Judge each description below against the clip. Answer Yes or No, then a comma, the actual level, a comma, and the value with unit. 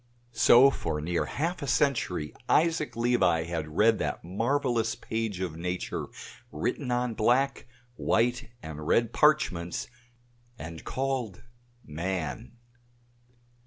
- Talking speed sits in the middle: No, slow, 110 wpm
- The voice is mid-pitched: No, low, 115 Hz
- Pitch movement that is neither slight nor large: No, wide, 7.1 semitones